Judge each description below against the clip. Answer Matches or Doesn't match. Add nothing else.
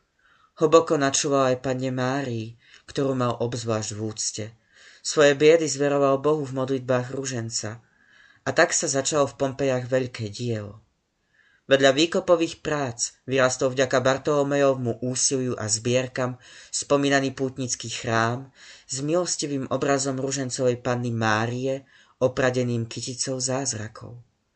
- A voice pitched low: Matches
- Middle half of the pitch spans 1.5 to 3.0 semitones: Matches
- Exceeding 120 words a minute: Doesn't match